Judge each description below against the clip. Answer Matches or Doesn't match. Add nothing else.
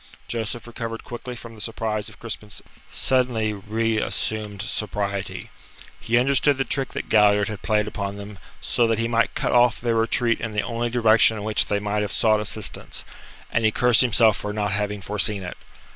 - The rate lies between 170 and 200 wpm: Matches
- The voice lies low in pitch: Matches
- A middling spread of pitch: Doesn't match